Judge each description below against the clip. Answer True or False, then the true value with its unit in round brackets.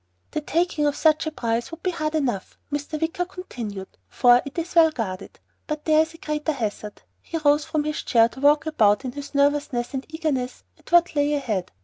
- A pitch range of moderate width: True (4.4 semitones)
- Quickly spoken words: True (210 wpm)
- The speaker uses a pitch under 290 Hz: False (295 Hz)